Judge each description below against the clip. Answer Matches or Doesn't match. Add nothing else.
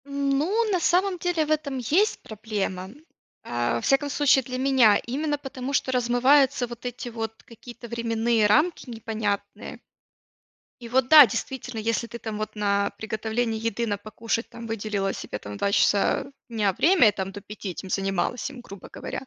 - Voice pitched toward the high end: Matches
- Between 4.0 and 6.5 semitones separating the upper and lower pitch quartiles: Matches